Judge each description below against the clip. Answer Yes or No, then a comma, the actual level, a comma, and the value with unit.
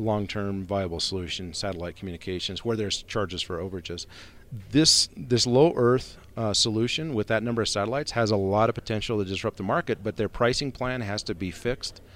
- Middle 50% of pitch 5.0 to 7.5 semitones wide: No, average, 3.5 semitones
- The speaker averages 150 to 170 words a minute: No, average, 190 wpm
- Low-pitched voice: Yes, low, 105 Hz